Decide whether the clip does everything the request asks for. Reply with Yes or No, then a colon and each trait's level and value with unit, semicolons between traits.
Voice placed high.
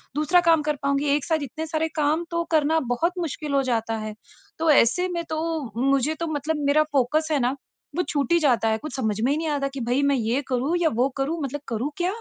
Yes: very high, 290 Hz